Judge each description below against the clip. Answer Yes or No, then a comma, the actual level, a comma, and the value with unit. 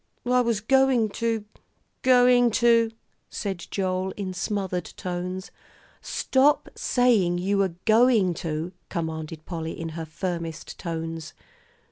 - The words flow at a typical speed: No, slow, 120 wpm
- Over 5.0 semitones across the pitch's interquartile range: Yes, wide, 5.5 semitones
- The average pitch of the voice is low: No, high, 190 Hz